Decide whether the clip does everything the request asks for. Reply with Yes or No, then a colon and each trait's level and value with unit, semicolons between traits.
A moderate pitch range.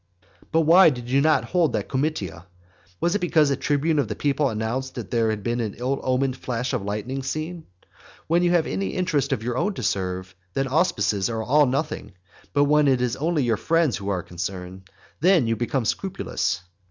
No: wide, 5.8 semitones